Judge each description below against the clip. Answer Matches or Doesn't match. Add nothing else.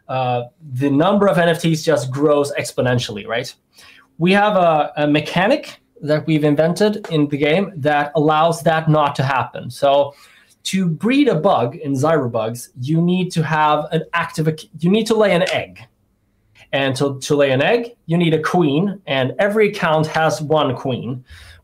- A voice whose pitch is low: Doesn't match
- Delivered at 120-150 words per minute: Doesn't match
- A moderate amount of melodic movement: Matches